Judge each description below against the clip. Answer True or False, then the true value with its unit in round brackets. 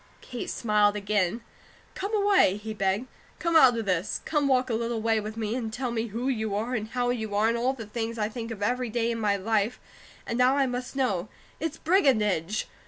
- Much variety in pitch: False (3.0 semitones)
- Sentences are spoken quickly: True (220 wpm)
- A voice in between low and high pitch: False (230 Hz)